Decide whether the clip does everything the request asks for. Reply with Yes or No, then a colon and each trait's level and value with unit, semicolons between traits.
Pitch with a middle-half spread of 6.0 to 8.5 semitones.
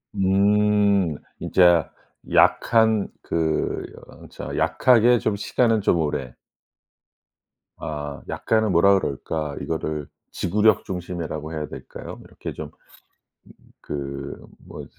No: average, 5.3 semitones